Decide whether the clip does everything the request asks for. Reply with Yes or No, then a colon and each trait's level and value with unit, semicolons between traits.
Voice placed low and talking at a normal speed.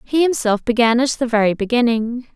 No: high, 240 Hz; average, 180 wpm